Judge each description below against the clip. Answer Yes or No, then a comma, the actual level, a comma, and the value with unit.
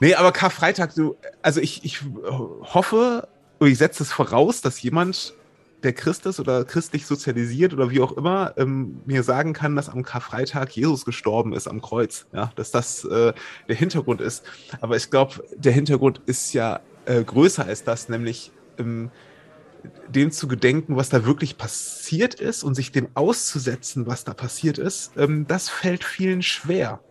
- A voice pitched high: No, medium, 140 Hz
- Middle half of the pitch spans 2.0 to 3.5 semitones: No, average, 4.8 semitones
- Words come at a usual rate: Yes, average, 170 wpm